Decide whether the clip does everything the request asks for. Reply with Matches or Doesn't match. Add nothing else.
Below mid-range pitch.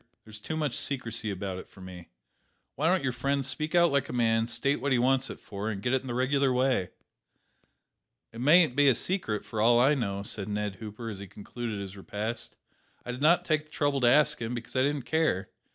Matches